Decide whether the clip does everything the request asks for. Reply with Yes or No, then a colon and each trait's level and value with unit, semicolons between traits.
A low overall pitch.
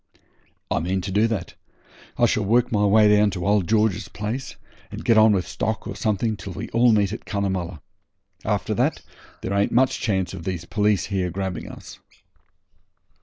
Yes: low, 100 Hz